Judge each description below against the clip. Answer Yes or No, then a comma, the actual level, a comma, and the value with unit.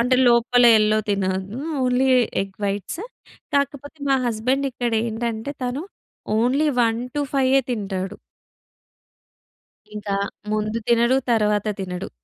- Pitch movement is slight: No, average, 3.6 semitones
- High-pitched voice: Yes, high, 235 Hz